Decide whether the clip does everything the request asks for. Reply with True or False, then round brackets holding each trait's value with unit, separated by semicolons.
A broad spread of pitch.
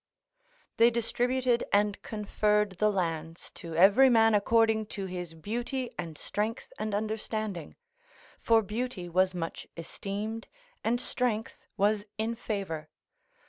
False (3.3 semitones)